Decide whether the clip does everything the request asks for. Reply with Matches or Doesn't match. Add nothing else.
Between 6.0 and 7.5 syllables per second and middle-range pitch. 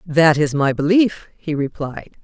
Doesn't match